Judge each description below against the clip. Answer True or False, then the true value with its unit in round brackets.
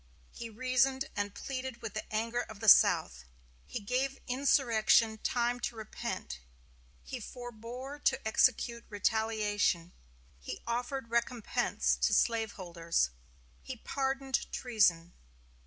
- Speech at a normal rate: False (110 wpm)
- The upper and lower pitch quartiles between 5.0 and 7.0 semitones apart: False (3.2 semitones)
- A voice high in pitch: True (235 Hz)